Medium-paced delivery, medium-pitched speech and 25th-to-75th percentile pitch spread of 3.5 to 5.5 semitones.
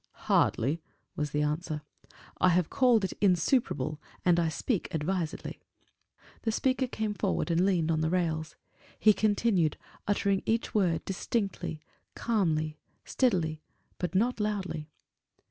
No: slow, 130 wpm; medium, 180 Hz; average, 4.8 semitones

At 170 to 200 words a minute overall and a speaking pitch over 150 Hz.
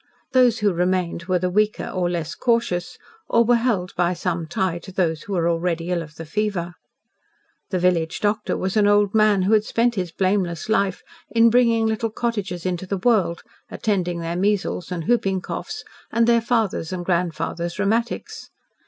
Yes: average, 180 wpm; high, 190 Hz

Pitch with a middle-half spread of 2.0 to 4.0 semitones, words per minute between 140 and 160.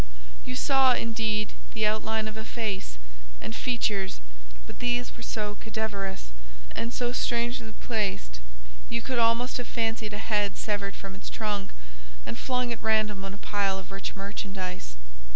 Yes: average, 2.8 semitones; average, 155 wpm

